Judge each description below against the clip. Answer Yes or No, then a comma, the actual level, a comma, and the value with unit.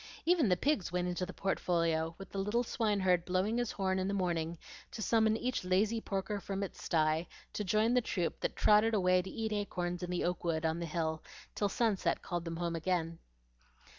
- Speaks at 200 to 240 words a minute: Yes, fast, 205 wpm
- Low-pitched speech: No, medium, 185 Hz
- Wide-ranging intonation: No, average, 3.5 semitones